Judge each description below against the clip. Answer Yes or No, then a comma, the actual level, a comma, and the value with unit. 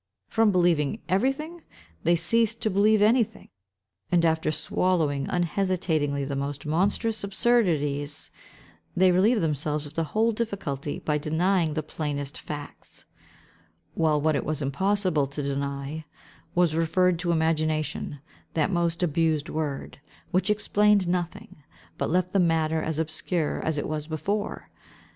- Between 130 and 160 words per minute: Yes, slow, 135 wpm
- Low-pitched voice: No, medium, 165 Hz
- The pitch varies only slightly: No, average, 4.2 semitones